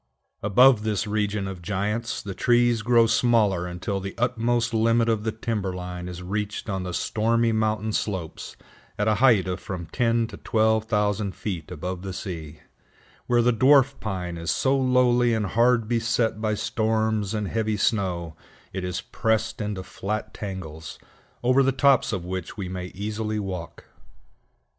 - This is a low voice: Yes, low, 105 Hz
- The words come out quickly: No, average, 160 wpm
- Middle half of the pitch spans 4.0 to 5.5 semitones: No, average, 3.5 semitones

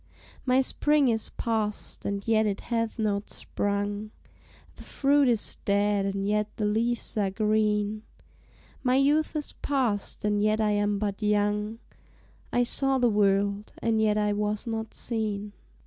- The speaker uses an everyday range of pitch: No, narrow, 2.0 semitones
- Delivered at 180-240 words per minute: No, average, 150 wpm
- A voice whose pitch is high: Yes, high, 210 Hz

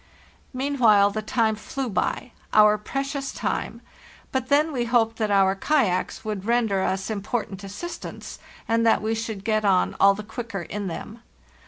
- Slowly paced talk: No, average, 160 wpm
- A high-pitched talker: Yes, high, 220 Hz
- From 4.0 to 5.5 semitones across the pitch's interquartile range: No, average, 3.3 semitones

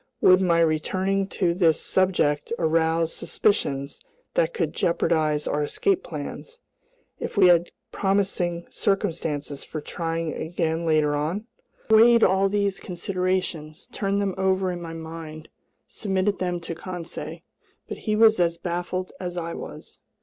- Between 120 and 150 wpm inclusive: Yes, average, 140 wpm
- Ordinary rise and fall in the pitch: Yes, average, 3.0 semitones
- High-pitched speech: No, medium, 175 Hz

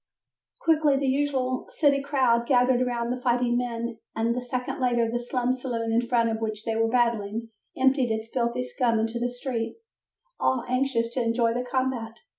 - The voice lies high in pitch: Yes, high, 245 Hz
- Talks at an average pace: Yes, average, 180 wpm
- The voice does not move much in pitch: Yes, narrow, 1.8 semitones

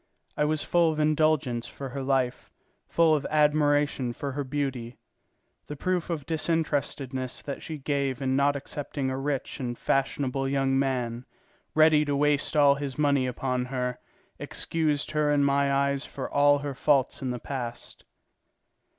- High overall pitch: No, medium, 140 Hz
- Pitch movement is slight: Yes, narrow, 2.1 semitones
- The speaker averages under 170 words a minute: Yes, average, 160 wpm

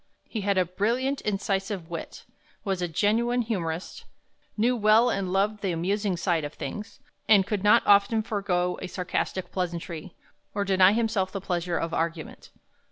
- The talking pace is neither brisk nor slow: Yes, average, 160 wpm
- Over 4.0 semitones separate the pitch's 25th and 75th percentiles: No, average, 3.0 semitones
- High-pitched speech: Yes, high, 195 Hz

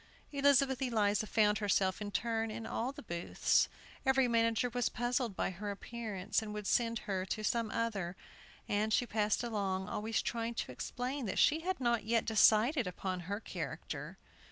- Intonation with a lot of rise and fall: No, average, 2.9 semitones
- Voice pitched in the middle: No, high, 225 Hz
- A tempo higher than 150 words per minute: Yes, average, 170 wpm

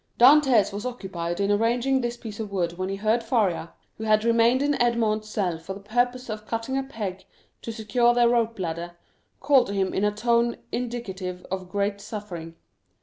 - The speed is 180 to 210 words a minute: Yes, average, 190 wpm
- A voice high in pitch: Yes, high, 215 Hz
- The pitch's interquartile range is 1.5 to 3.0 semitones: No, average, 3.6 semitones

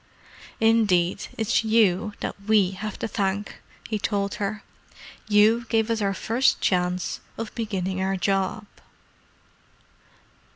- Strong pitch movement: No, narrow, 2.6 semitones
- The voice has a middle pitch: No, high, 205 Hz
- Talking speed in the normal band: No, slow, 120 wpm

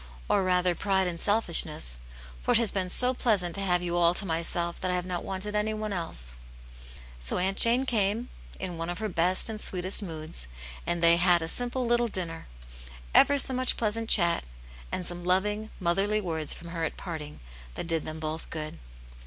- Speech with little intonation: No, average, 3.8 semitones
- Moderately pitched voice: Yes, medium, 180 Hz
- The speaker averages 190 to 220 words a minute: Yes, average, 195 wpm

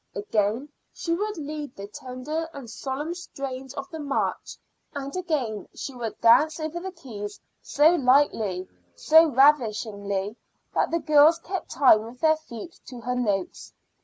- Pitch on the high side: Yes, very high, 275 Hz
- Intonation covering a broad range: Yes, wide, 5.8 semitones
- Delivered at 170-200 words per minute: No, average, 150 wpm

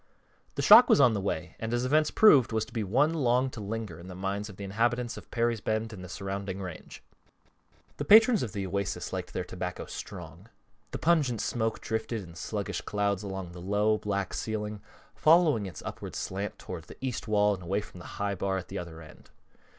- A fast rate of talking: Yes, fast, 210 wpm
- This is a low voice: Yes, low, 105 Hz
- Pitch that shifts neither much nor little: Yes, average, 3.7 semitones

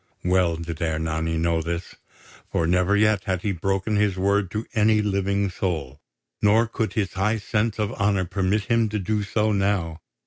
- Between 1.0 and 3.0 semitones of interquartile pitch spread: No, average, 3.5 semitones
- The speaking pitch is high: No, low, 100 Hz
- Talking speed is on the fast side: No, average, 175 wpm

